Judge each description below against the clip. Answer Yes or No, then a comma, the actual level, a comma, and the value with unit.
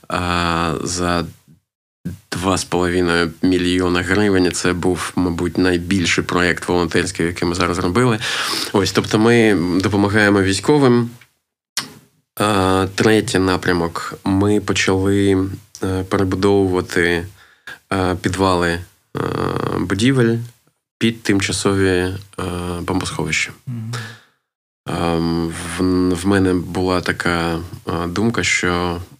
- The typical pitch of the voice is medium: No, very low, 95 Hz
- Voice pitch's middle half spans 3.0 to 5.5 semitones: No, narrow, 2.5 semitones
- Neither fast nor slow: No, slow, 75 wpm